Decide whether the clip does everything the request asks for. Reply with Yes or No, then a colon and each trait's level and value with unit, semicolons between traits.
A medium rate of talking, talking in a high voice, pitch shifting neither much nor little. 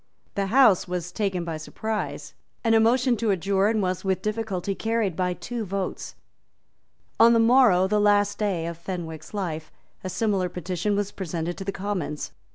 Yes: average, 165 wpm; high, 195 Hz; average, 3.2 semitones